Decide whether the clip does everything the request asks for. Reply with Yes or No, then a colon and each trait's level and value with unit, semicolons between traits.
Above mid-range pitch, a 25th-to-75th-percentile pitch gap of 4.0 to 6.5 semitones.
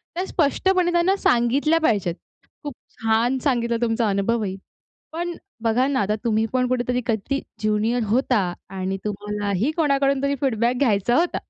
Yes: high, 240 Hz; average, 4.6 semitones